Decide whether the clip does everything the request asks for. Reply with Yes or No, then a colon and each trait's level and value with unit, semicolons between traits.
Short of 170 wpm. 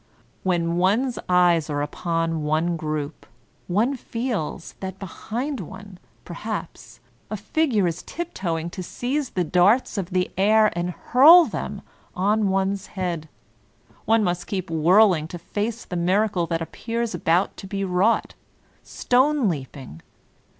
Yes: average, 140 wpm